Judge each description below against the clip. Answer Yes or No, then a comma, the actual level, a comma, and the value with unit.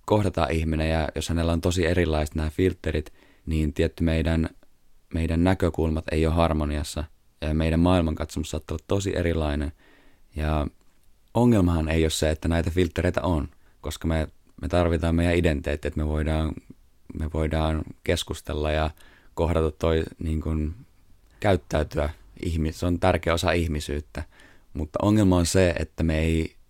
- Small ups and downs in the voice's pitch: Yes, narrow, 2.0 semitones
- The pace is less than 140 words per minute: No, average, 145 wpm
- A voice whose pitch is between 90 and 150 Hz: No, very low, 80 Hz